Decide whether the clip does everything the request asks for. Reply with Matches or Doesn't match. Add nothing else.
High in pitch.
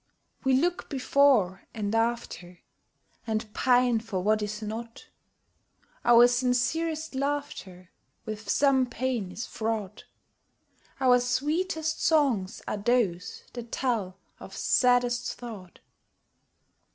Matches